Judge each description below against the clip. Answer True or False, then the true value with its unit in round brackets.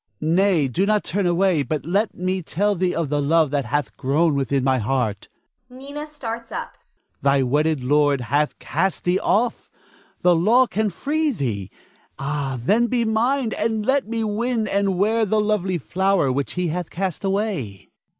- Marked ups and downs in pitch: True (7.3 semitones)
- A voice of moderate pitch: True (180 Hz)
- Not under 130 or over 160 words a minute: False (170 wpm)